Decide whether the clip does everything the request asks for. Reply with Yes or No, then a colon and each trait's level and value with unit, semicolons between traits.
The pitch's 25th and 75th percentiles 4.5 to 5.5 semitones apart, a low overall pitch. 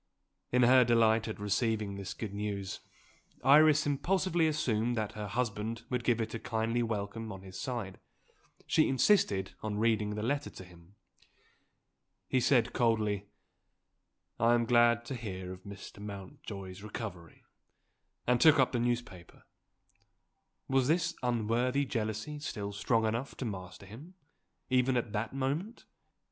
No: average, 3.5 semitones; low, 115 Hz